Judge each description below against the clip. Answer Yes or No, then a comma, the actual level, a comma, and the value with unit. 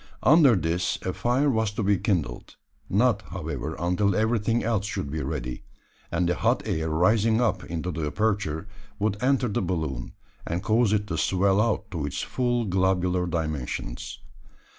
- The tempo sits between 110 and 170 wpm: Yes, average, 160 wpm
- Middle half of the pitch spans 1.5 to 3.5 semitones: No, average, 5.1 semitones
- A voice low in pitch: Yes, very low, 95 Hz